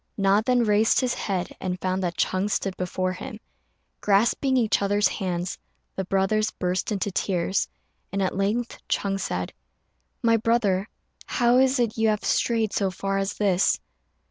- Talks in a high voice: Yes, high, 200 Hz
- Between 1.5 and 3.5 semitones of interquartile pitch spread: Yes, average, 3.0 semitones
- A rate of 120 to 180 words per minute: Yes, average, 160 wpm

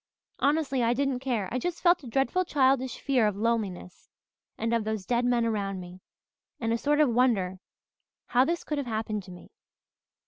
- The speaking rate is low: No, average, 185 wpm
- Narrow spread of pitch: No, average, 4.1 semitones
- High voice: Yes, high, 240 Hz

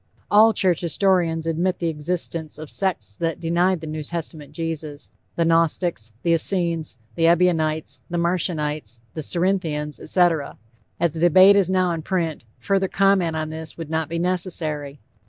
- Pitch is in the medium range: Yes, medium, 165 Hz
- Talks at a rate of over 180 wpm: No, average, 155 wpm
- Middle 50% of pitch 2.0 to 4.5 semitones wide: Yes, narrow, 2.5 semitones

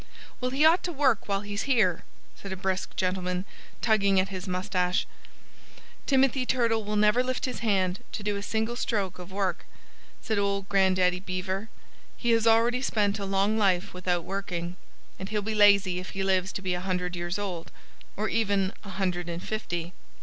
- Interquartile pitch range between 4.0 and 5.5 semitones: No, average, 3.0 semitones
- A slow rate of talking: No, average, 185 wpm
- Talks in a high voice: Yes, high, 195 Hz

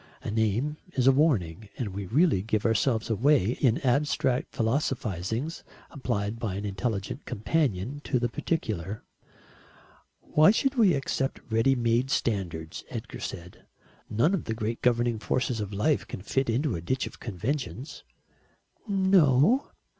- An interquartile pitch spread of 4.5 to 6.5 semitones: Yes, average, 5.2 semitones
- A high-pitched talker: No, low, 120 Hz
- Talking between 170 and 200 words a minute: No, average, 140 wpm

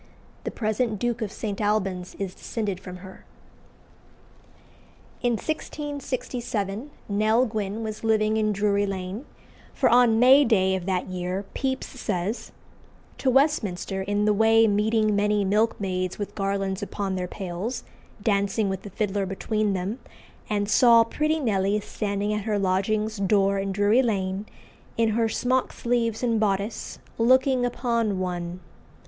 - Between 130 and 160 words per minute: Yes, average, 140 wpm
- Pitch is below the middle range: No, high, 210 Hz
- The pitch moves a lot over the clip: No, average, 2.8 semitones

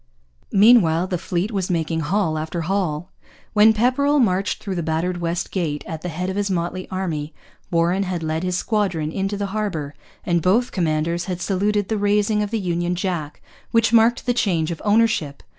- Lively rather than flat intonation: No, average, 3.7 semitones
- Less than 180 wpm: No, average, 185 wpm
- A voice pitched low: No, medium, 185 Hz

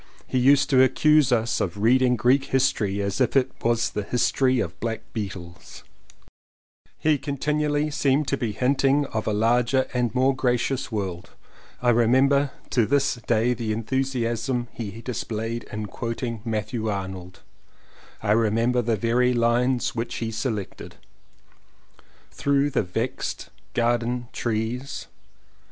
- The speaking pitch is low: Yes, low, 120 Hz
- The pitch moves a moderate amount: Yes, average, 3.0 semitones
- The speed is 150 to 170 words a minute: No, slow, 135 wpm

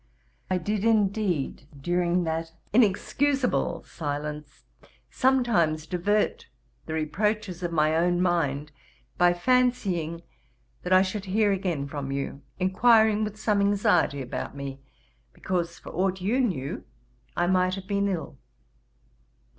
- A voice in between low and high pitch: Yes, medium, 180 Hz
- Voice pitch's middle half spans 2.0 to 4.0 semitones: No, average, 4.5 semitones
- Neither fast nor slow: No, slow, 125 wpm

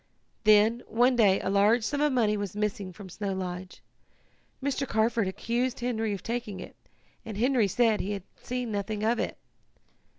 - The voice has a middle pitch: No, high, 220 Hz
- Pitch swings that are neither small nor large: Yes, average, 3.2 semitones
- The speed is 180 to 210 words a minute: No, average, 170 wpm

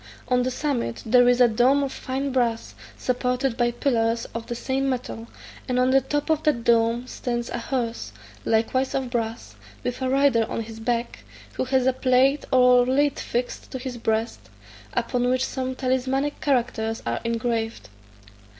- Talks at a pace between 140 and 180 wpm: Yes, average, 170 wpm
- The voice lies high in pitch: Yes, very high, 250 Hz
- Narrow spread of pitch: Yes, narrow, 2.1 semitones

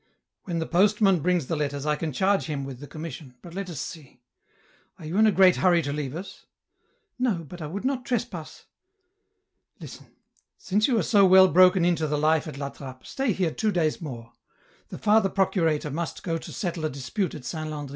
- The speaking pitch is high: No, medium, 170 Hz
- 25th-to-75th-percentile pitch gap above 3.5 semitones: Yes, average, 4.7 semitones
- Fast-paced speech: Yes, fast, 225 wpm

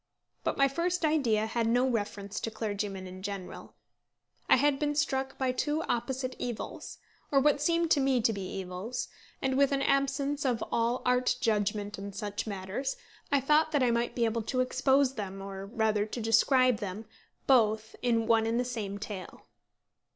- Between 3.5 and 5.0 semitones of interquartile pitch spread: Yes, average, 4.5 semitones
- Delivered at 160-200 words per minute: Yes, average, 180 wpm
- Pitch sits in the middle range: No, high, 235 Hz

